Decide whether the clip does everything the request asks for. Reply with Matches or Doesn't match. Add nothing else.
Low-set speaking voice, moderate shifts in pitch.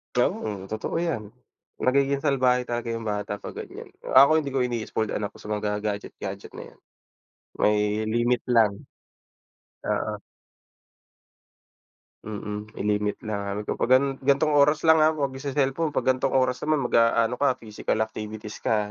Matches